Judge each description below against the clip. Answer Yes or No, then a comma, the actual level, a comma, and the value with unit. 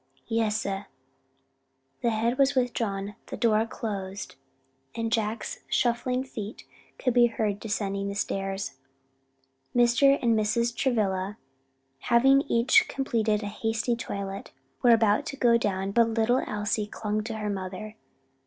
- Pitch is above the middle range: Yes, high, 220 Hz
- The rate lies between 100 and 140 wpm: Yes, slow, 135 wpm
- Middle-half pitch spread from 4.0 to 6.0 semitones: No, narrow, 2.6 semitones